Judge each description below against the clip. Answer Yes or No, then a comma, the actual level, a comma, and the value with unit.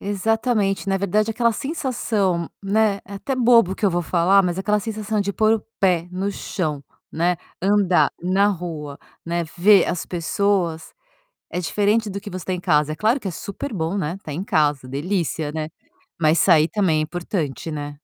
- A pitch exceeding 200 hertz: No, high, 190 Hz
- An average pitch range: Yes, average, 3.9 semitones